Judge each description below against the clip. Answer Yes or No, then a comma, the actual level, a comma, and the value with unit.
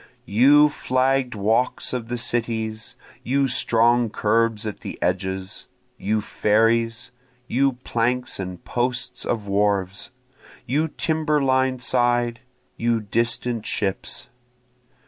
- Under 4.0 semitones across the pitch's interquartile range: Yes, average, 2.8 semitones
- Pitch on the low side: Yes, low, 120 Hz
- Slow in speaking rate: Yes, slow, 105 wpm